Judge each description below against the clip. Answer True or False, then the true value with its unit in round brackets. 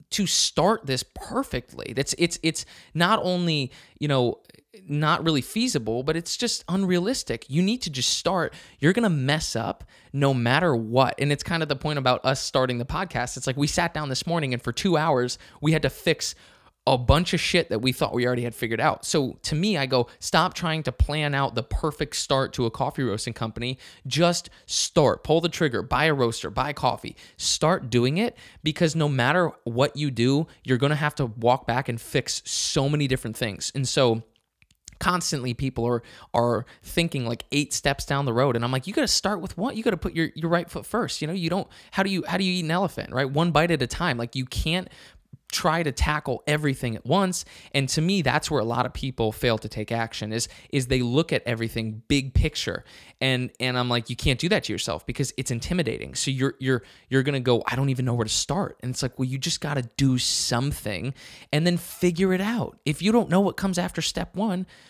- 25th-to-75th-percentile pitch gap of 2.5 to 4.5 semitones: False (5.2 semitones)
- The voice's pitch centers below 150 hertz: True (140 Hz)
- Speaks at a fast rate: True (230 wpm)